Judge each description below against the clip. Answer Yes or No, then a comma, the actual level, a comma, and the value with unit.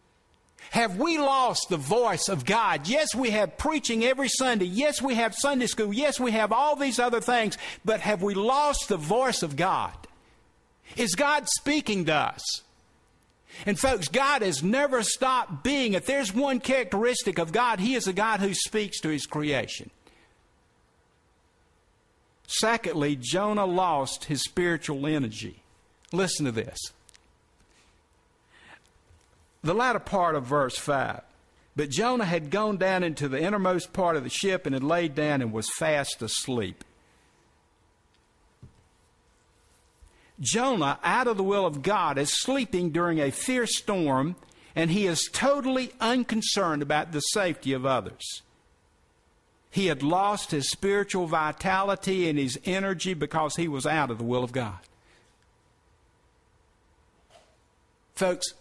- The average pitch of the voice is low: No, medium, 180 Hz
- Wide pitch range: Yes, wide, 8.5 semitones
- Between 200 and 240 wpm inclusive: No, average, 140 wpm